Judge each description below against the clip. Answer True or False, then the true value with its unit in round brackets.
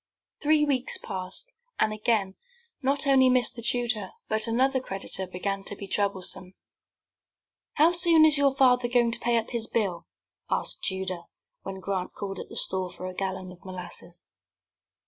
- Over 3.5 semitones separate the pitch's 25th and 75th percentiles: True (5.3 semitones)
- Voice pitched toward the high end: True (215 Hz)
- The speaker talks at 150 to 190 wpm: True (160 wpm)